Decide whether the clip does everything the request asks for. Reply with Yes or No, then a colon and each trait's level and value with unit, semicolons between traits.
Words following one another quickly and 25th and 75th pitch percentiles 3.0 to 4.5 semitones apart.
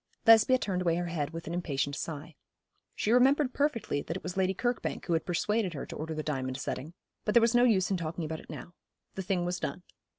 No: fast, 235 wpm; wide, 5.6 semitones